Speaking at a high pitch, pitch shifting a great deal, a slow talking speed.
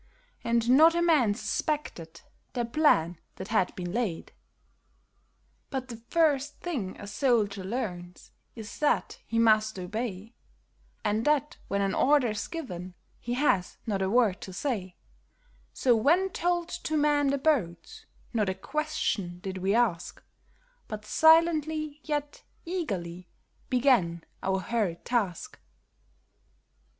Yes: high, 230 Hz; wide, 7.6 semitones; slow, 125 wpm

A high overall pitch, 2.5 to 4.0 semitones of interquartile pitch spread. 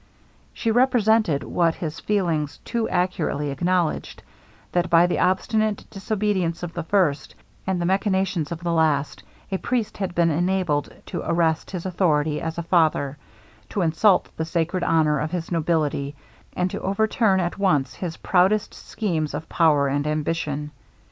No: medium, 170 Hz; average, 3.5 semitones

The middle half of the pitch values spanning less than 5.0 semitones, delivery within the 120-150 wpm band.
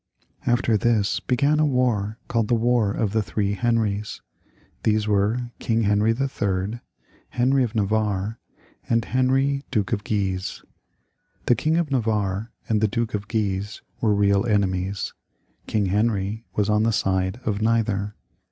Yes: average, 2.8 semitones; average, 145 wpm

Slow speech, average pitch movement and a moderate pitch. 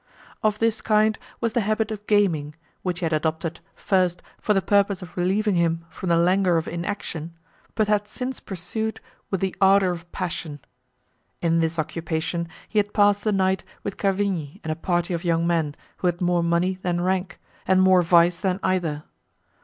No: average, 185 wpm; average, 3.1 semitones; medium, 180 Hz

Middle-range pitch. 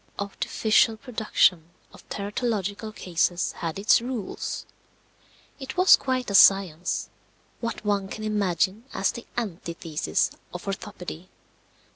No: high, 200 Hz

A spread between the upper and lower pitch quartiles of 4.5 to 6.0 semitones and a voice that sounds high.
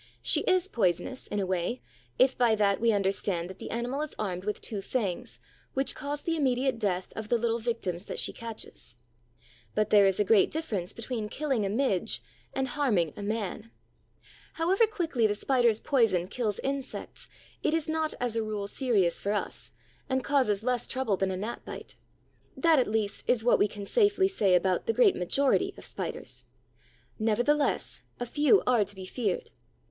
Yes: average, 4.9 semitones; high, 230 Hz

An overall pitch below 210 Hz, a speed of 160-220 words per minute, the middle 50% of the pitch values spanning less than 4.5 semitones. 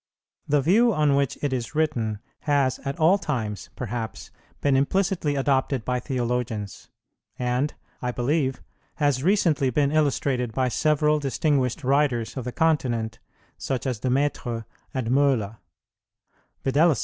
No: low, 135 Hz; slow, 135 wpm; average, 3.1 semitones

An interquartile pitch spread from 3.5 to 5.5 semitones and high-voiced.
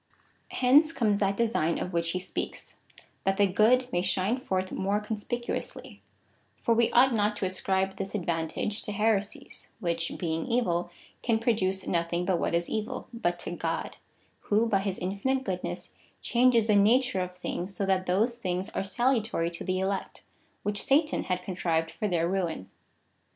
Yes: average, 3.9 semitones; high, 195 Hz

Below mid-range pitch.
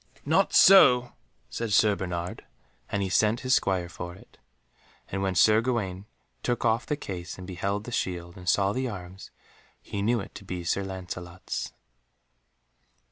Yes: low, 100 Hz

